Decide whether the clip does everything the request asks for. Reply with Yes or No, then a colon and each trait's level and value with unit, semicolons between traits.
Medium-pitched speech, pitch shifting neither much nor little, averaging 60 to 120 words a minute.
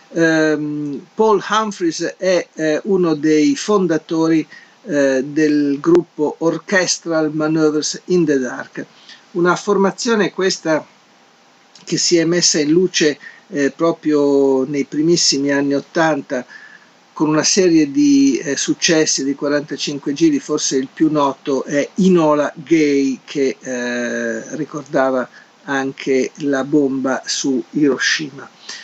Yes: medium, 155 Hz; average, 3.7 semitones; slow, 115 wpm